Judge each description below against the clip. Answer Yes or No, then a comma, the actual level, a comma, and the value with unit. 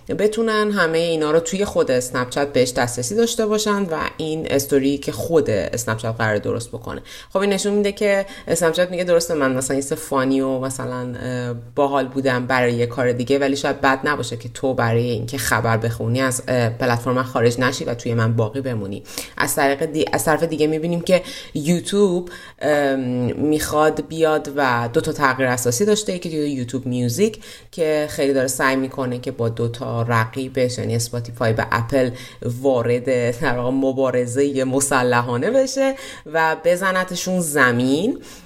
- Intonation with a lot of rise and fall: No, average, 4.5 semitones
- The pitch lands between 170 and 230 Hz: No, low, 135 Hz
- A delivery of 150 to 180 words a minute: Yes, fast, 155 wpm